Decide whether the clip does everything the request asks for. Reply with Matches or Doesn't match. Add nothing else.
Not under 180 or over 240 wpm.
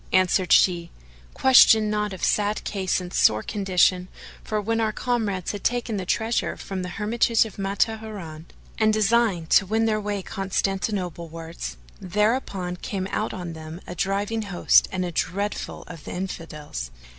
Doesn't match